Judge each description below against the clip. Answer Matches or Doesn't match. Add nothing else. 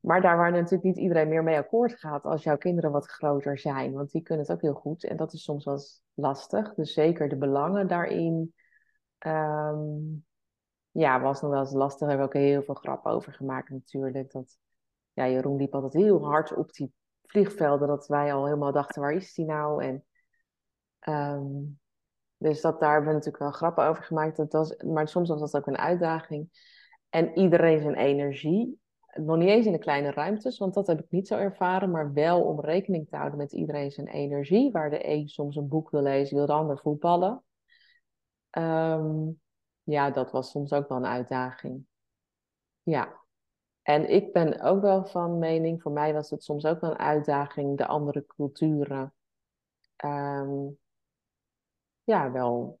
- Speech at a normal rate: Matches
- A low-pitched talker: Doesn't match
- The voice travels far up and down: Doesn't match